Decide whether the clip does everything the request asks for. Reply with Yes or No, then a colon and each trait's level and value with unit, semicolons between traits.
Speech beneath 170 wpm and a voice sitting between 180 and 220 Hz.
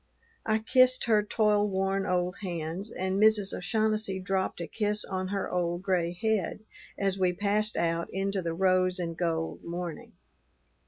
Yes: average, 150 wpm; high, 190 Hz